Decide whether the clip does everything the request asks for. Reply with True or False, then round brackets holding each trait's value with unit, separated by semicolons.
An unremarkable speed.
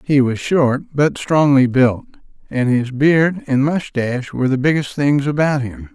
True (170 wpm)